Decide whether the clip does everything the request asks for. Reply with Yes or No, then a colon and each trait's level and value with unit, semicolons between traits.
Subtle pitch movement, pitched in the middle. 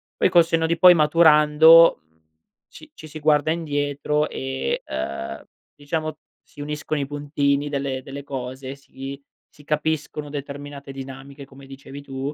Yes: narrow, 1.9 semitones; medium, 145 Hz